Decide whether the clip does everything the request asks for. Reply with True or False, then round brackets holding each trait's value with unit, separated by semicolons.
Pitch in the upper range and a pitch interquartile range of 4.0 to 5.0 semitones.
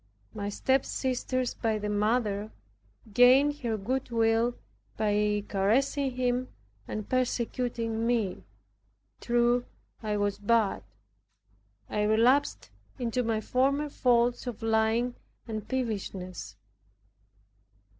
False (230 Hz; 2.9 semitones)